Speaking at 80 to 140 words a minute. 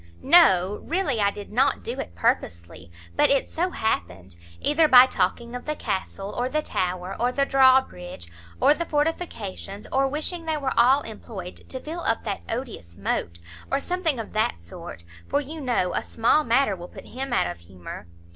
No: average, 185 wpm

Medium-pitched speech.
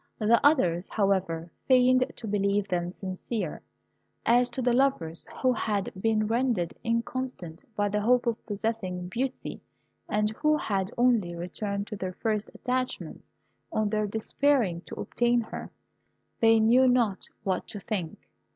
No: high, 215 Hz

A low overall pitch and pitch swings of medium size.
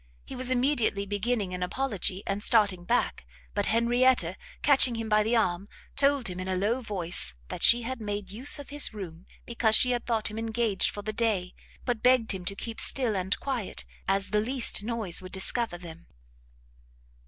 No: high, 215 Hz; average, 4.0 semitones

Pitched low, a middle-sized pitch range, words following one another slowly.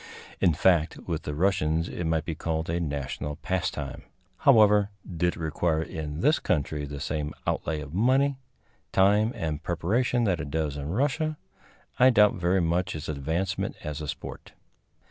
No: very low, 85 Hz; average, 4.4 semitones; average, 165 wpm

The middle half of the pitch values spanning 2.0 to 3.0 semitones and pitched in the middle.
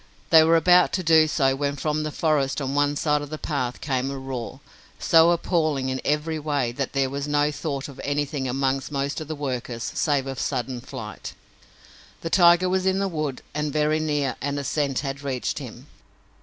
Yes: narrow, 2.6 semitones; medium, 145 Hz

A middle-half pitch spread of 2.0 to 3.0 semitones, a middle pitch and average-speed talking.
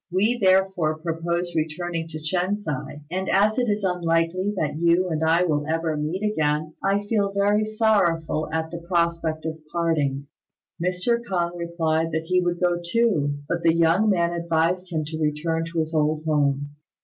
Yes: average, 2.7 semitones; medium, 170 Hz; average, 175 wpm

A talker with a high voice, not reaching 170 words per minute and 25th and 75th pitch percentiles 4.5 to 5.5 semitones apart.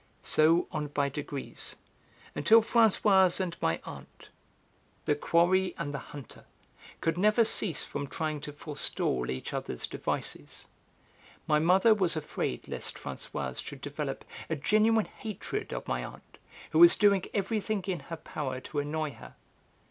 No: medium, 165 Hz; average, 145 wpm; average, 5.1 semitones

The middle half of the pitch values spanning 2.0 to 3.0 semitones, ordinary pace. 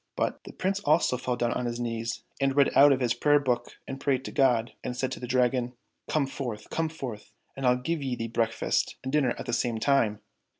No: narrow, 2.5 semitones; fast, 240 wpm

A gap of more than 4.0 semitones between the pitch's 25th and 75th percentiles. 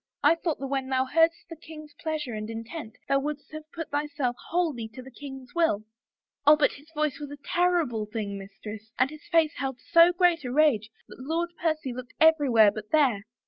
Yes: average, 4.6 semitones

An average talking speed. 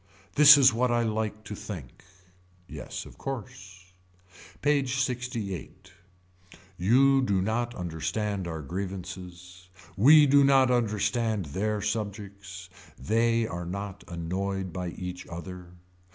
No: slow, 115 wpm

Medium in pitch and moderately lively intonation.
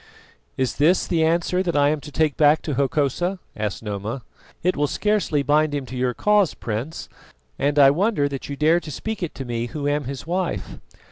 Yes: medium, 145 Hz; average, 4.0 semitones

